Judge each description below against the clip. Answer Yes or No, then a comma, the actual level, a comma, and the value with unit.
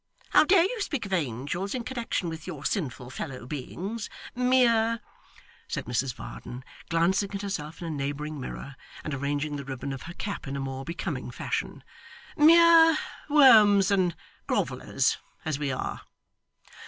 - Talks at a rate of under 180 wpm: Yes, average, 155 wpm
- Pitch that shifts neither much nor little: No, wide, 8.6 semitones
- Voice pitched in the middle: Yes, medium, 170 Hz